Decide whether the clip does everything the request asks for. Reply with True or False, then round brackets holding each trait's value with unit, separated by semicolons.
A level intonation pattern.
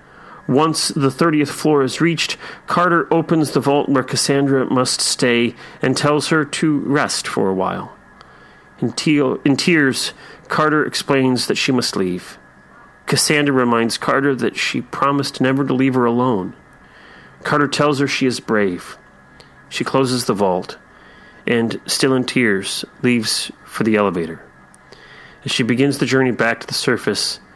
False (3.3 semitones)